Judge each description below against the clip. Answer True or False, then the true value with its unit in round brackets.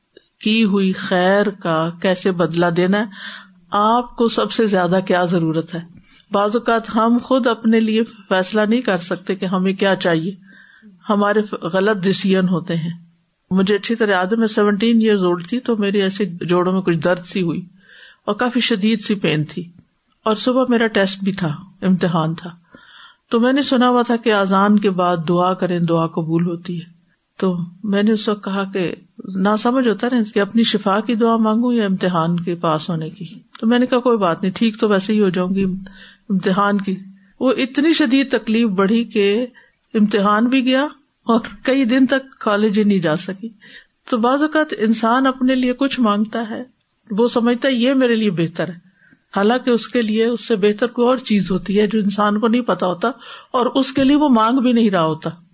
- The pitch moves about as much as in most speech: True (4.1 semitones)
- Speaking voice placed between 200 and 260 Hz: True (210 Hz)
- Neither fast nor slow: False (200 wpm)